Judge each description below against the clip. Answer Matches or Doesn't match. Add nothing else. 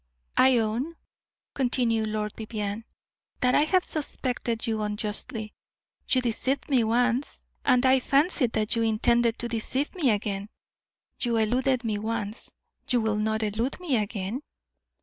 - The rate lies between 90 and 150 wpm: Matches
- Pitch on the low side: Doesn't match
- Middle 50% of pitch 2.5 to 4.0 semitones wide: Matches